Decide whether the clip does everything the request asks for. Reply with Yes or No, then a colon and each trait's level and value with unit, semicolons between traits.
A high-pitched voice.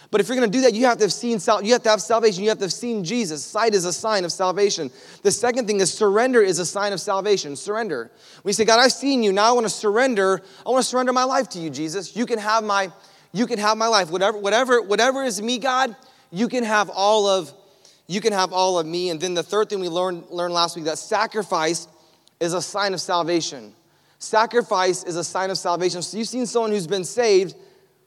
Yes: high, 205 Hz